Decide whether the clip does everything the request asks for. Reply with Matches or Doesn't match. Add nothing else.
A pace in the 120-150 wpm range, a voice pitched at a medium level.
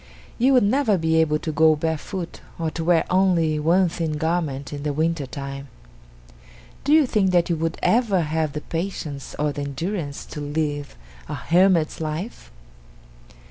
Doesn't match